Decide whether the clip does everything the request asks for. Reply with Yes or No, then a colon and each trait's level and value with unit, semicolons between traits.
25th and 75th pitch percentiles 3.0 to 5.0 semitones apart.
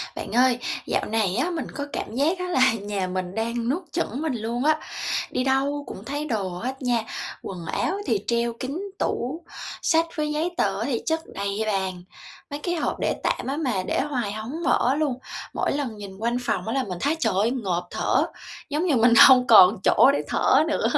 No: wide, 5.4 semitones